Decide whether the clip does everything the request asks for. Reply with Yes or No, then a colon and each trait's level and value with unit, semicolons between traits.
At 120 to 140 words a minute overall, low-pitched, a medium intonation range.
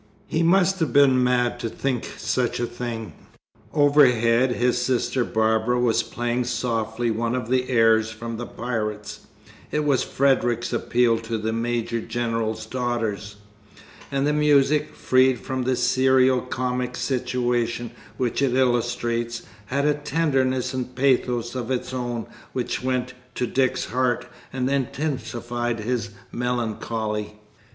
No: slow, 135 wpm; low, 125 Hz; narrow, 1.9 semitones